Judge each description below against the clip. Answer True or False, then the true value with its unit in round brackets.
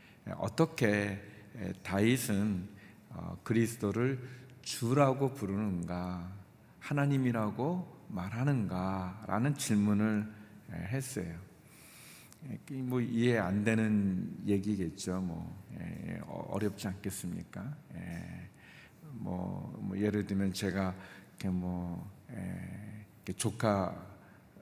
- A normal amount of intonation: True (4.4 semitones)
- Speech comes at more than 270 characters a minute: False (180 characters per minute)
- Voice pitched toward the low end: True (105 Hz)